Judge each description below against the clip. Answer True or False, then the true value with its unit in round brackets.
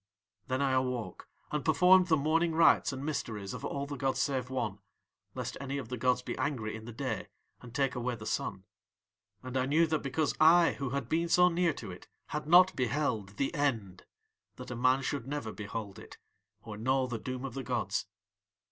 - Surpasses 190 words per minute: True (200 wpm)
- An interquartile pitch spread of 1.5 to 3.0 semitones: False (4.0 semitones)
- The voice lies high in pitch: False (130 Hz)